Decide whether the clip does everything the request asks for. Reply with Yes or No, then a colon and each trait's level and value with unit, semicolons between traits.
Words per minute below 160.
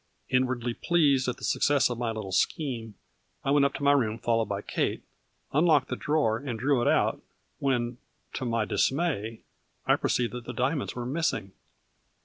No: average, 175 wpm